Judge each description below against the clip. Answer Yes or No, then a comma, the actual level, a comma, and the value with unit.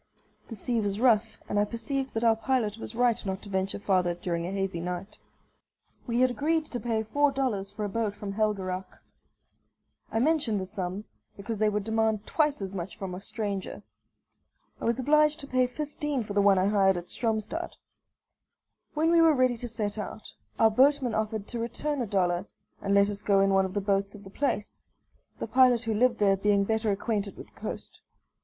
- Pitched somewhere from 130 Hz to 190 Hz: No, high, 215 Hz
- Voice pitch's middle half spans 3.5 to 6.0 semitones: Yes, average, 3.8 semitones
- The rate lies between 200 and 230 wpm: Yes, fast, 205 wpm